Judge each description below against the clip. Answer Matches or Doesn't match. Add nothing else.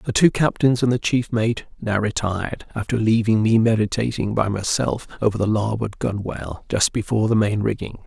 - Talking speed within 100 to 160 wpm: Doesn't match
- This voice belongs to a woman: Doesn't match